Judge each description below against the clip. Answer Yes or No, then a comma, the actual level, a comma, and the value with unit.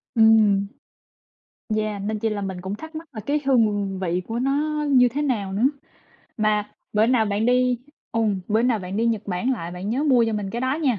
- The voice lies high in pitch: Yes, high, 220 Hz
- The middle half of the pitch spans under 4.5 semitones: Yes, average, 3.8 semitones